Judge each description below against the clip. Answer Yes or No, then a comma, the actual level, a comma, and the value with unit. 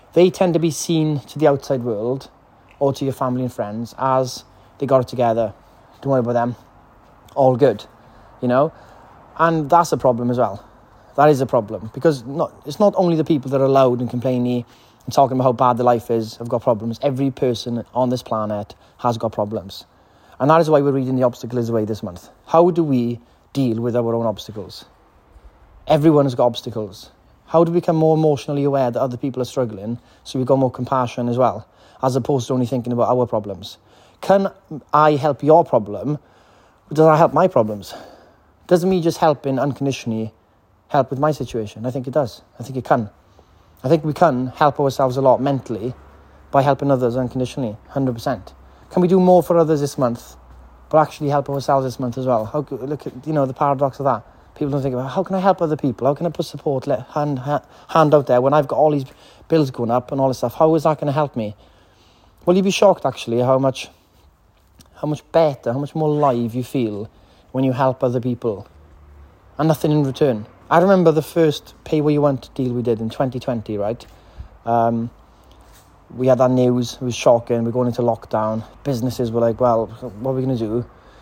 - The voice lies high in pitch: No, low, 125 Hz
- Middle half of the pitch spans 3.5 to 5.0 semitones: Yes, average, 4.2 semitones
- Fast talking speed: Yes, fast, 210 wpm